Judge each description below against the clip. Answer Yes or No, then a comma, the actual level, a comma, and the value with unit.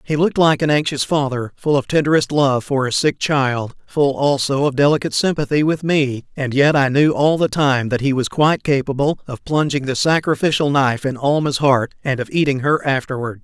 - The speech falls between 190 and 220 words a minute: Yes, average, 200 wpm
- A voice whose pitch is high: No, medium, 140 Hz